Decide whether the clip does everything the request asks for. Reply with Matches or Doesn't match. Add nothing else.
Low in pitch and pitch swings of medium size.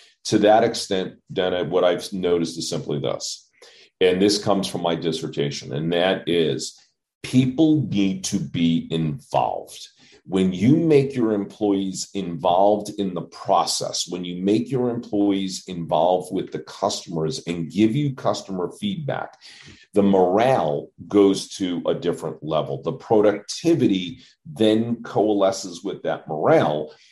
Matches